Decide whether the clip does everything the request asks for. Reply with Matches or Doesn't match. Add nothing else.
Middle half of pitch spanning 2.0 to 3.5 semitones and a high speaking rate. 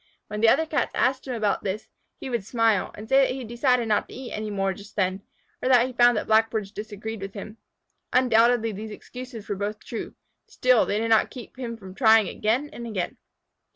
Matches